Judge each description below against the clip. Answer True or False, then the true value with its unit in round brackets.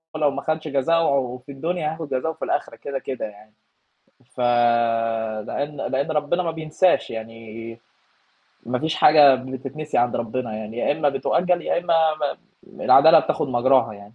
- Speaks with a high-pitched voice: False (140 Hz)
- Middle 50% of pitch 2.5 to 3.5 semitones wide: False (4.4 semitones)